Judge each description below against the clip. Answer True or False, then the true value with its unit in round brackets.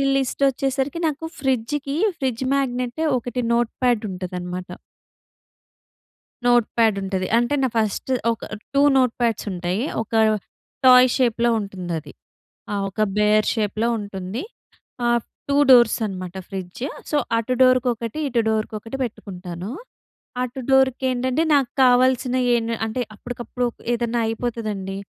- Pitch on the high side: True (235 Hz)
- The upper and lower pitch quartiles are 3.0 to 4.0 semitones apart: True (3.6 semitones)